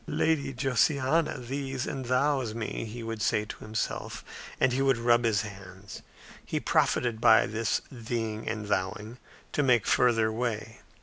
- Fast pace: No, average, 150 wpm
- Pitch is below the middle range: Yes, low, 115 Hz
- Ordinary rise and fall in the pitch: Yes, average, 3.0 semitones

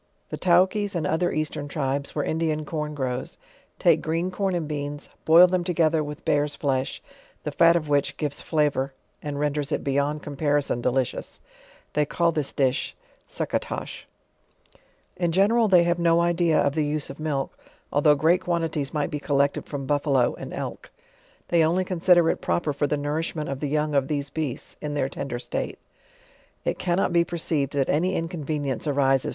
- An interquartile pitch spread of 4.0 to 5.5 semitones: No, average, 3.0 semitones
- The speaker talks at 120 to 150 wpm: No, average, 175 wpm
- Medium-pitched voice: Yes, medium, 150 Hz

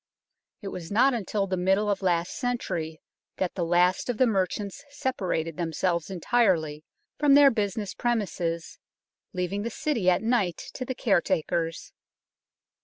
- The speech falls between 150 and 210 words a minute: No, average, 140 wpm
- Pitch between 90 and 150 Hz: No, high, 190 Hz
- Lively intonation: No, average, 5.0 semitones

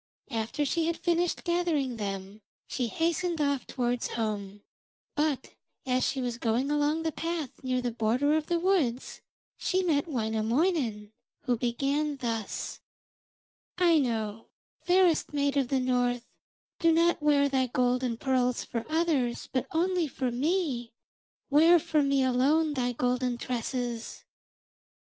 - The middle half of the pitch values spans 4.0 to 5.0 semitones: Yes, average, 4.7 semitones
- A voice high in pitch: Yes, very high, 265 Hz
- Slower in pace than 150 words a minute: Yes, slow, 135 wpm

